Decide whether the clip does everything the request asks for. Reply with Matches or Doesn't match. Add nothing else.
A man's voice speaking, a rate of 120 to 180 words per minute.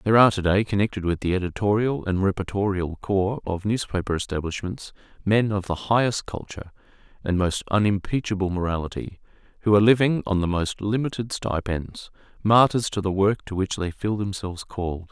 Matches